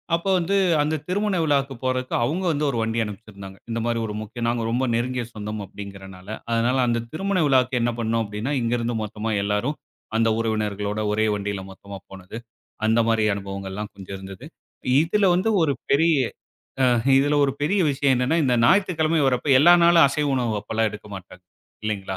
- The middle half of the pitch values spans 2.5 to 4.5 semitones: No, average, 5.3 semitones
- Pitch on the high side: No, low, 115 Hz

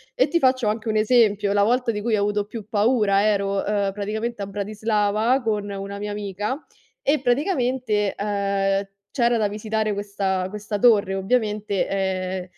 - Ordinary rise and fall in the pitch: No, narrow, 2.3 semitones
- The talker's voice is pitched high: Yes, high, 210 Hz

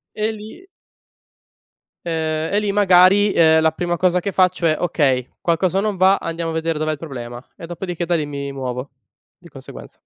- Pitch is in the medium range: Yes, medium, 170 Hz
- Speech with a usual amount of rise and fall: Yes, average, 3.2 semitones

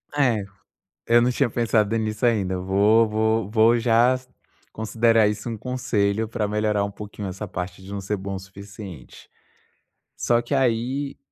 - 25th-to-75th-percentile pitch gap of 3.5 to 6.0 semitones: No, narrow, 2.6 semitones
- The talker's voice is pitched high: No, low, 110 Hz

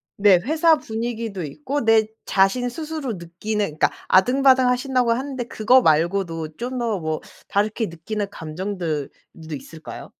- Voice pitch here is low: No, high, 215 Hz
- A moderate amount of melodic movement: No, wide, 6.6 semitones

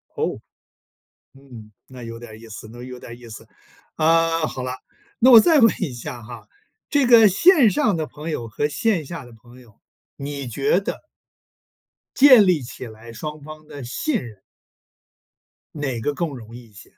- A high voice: No, medium, 140 Hz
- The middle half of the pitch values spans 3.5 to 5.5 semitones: No, wide, 6.3 semitones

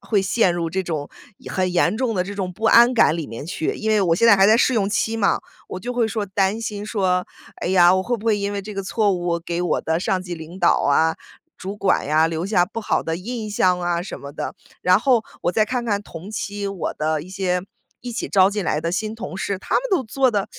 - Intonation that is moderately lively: Yes, average, 3.5 semitones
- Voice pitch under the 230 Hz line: Yes, high, 195 Hz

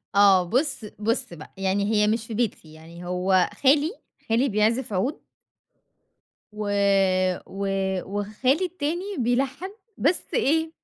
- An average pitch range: No, wide, 6.1 semitones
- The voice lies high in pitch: Yes, high, 225 Hz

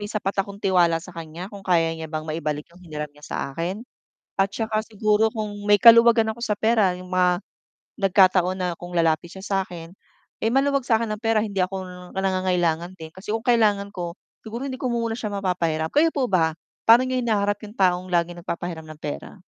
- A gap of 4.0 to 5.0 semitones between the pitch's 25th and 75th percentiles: Yes, average, 4.3 semitones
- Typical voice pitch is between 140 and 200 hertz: Yes, high, 190 Hz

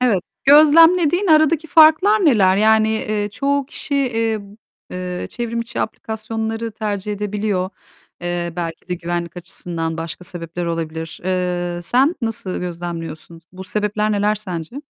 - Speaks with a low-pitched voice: No, high, 210 Hz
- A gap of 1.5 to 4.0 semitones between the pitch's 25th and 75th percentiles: No, average, 5.1 semitones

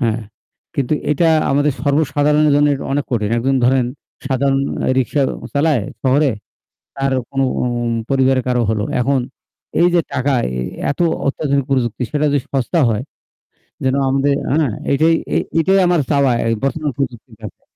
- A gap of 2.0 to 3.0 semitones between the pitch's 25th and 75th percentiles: Yes, narrow, 2.4 semitones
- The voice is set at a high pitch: No, low, 135 Hz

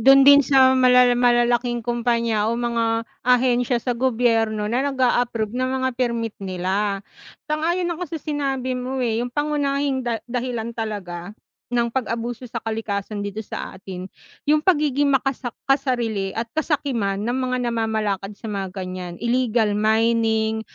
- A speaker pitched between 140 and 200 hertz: No, high, 235 Hz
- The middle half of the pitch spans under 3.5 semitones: Yes, average, 2.9 semitones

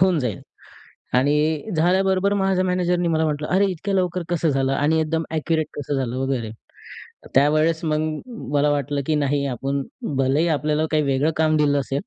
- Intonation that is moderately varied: Yes, average, 3.3 semitones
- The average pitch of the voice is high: No, medium, 155 Hz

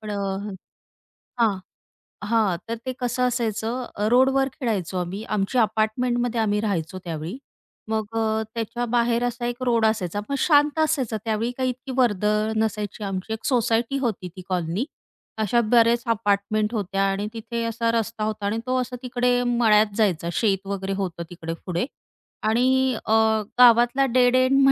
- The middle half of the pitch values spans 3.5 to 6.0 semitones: No, average, 2.9 semitones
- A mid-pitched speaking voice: No, high, 225 Hz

